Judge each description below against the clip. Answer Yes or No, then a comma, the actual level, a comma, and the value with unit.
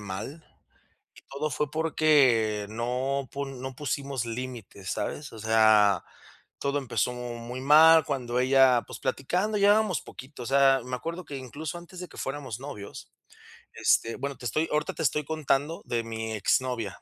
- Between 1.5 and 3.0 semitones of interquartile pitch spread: No, average, 4.1 semitones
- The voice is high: No, low, 130 Hz